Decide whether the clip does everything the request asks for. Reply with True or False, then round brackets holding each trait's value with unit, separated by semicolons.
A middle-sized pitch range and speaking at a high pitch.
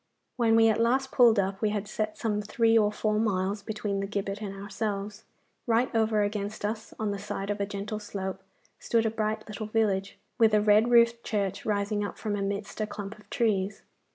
False (1.7 semitones; 210 Hz)